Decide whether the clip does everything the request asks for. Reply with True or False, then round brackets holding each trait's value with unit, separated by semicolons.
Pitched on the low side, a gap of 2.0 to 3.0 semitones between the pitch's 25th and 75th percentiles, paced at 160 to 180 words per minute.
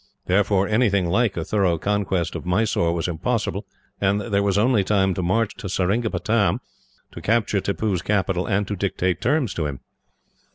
True (100 Hz; 2.7 semitones; 165 wpm)